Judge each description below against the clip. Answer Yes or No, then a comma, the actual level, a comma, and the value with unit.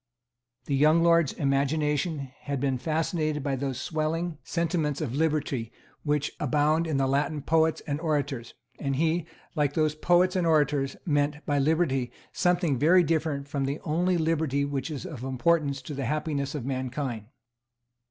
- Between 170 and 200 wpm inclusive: No, average, 155 wpm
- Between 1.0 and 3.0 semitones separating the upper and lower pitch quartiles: Yes, average, 2.7 semitones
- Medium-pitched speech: Yes, medium, 150 Hz